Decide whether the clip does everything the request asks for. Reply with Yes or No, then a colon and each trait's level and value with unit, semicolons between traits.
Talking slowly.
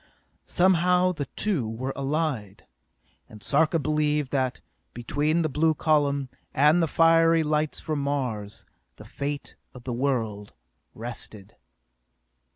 Yes: slow, 120 wpm